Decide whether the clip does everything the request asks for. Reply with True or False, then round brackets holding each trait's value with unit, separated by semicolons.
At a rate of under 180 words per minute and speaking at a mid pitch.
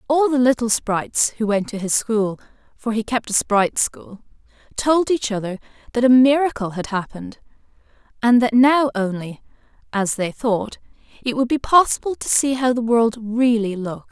False (165 wpm; 230 Hz)